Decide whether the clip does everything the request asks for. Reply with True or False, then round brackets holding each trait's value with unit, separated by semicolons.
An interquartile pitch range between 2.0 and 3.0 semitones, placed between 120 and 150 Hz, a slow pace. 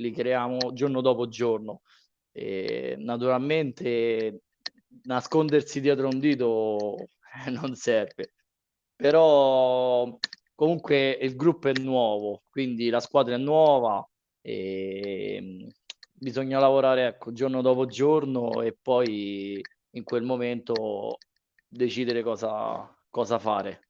True (2.6 semitones; 125 Hz; 100 wpm)